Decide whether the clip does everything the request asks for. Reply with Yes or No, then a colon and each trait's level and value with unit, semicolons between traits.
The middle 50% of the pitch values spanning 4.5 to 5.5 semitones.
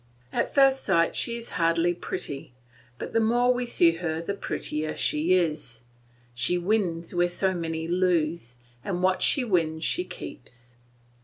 No: average, 3.0 semitones